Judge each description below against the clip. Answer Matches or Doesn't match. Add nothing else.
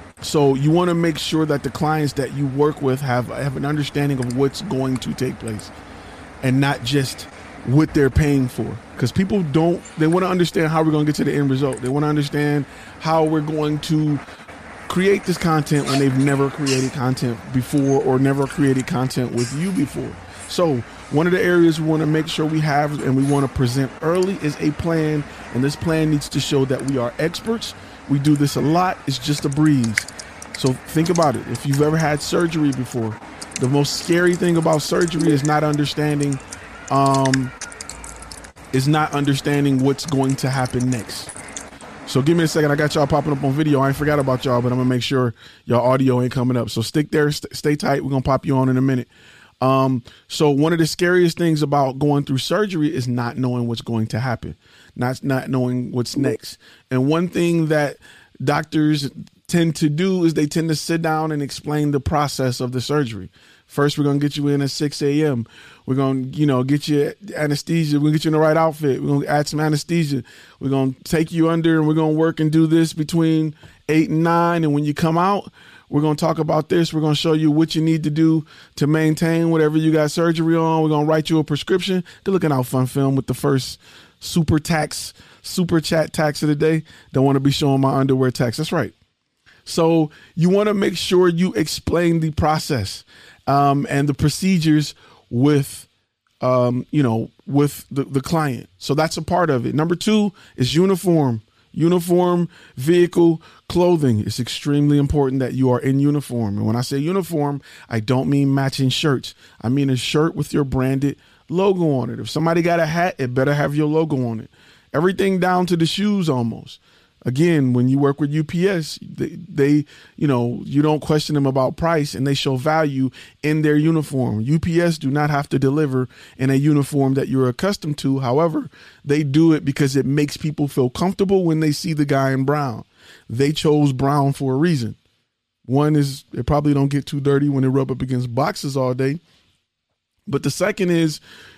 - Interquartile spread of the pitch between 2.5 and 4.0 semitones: Matches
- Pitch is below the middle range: Doesn't match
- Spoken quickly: Matches